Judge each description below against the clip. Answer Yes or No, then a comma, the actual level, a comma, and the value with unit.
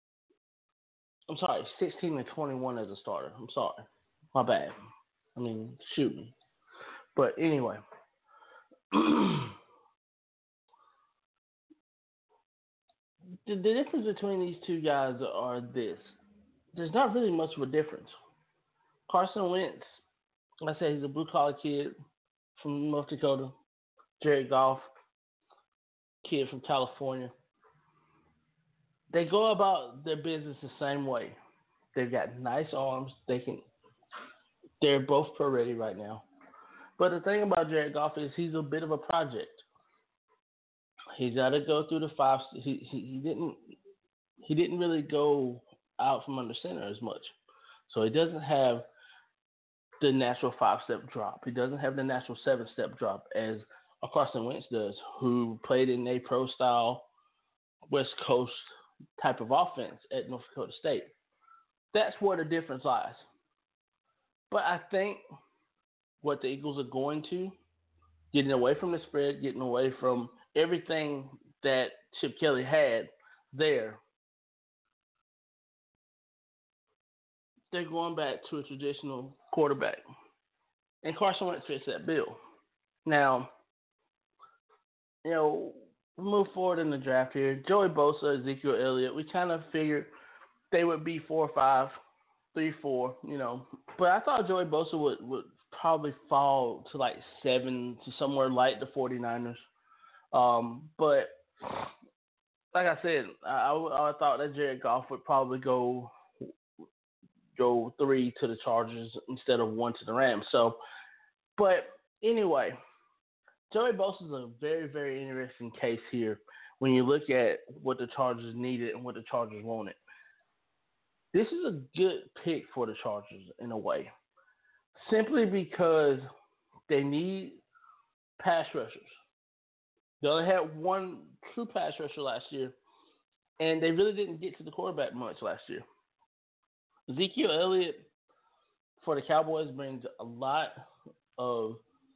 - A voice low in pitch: No, medium, 150 Hz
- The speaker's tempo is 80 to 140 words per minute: Yes, slow, 135 wpm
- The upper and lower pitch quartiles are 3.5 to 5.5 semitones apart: No, wide, 6.2 semitones